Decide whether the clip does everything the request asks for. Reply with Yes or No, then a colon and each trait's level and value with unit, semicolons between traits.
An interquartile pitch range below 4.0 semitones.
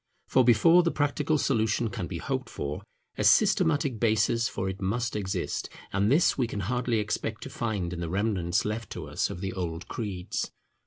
No: average, 4.4 semitones